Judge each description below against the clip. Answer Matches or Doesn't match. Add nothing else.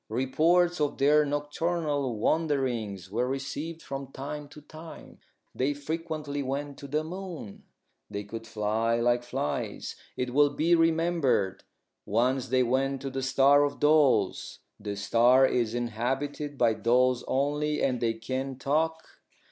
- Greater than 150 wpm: Doesn't match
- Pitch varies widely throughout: Doesn't match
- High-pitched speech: Doesn't match